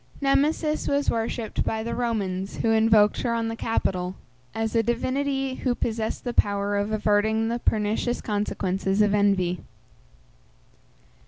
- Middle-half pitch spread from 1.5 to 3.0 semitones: Yes, average, 2.7 semitones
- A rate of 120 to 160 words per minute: Yes, average, 140 wpm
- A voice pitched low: No, high, 220 Hz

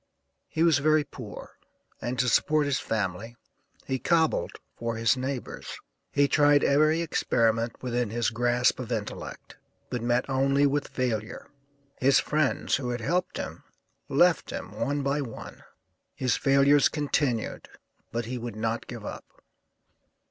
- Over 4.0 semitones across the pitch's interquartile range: No, average, 3.5 semitones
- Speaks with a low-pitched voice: Yes, low, 130 Hz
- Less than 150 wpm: Yes, average, 140 wpm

